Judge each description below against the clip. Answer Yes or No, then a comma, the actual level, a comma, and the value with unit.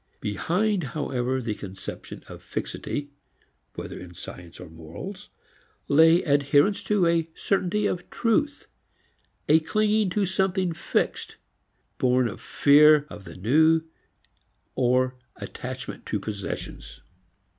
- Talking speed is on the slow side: Yes, slow, 115 wpm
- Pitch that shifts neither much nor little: No, wide, 7.2 semitones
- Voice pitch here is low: No, medium, 150 Hz